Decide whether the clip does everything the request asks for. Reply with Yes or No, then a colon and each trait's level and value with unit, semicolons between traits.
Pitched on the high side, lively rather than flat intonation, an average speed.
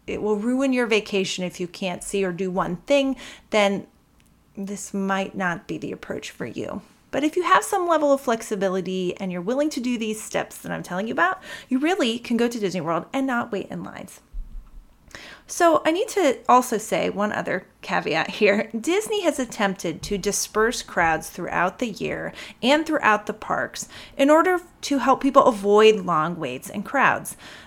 Yes: high, 215 Hz; wide, 5.8 semitones; average, 190 wpm